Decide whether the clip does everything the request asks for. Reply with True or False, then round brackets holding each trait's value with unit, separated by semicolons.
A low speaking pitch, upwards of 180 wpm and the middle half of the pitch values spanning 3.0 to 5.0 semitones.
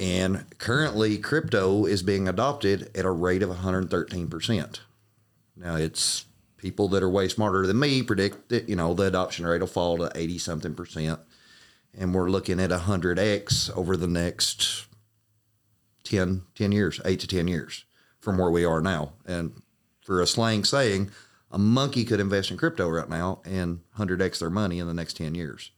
False (95 Hz; 170 wpm; 3.3 semitones)